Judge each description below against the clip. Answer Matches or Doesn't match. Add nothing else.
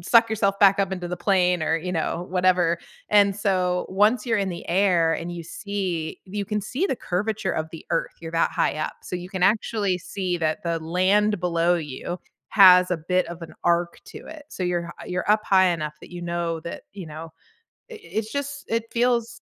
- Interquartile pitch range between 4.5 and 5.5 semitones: Doesn't match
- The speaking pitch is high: Doesn't match